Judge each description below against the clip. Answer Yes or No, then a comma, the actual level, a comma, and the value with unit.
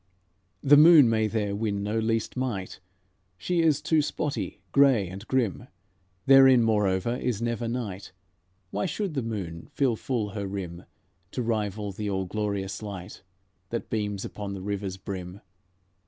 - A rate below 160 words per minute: Yes, average, 150 wpm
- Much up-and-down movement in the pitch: No, average, 4.0 semitones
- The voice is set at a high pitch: No, low, 105 Hz